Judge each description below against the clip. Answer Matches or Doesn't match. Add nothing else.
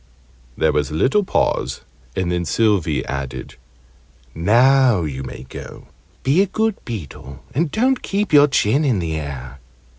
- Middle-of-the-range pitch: Doesn't match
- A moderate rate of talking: Matches